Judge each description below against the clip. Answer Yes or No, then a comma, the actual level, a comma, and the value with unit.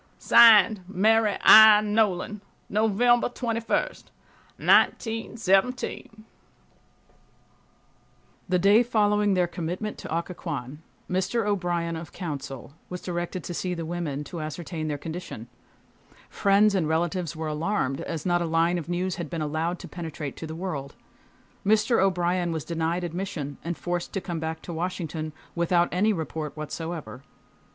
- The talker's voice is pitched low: No, medium, 175 Hz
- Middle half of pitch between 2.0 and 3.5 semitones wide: No, average, 4.0 semitones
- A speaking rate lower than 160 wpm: Yes, slow, 135 wpm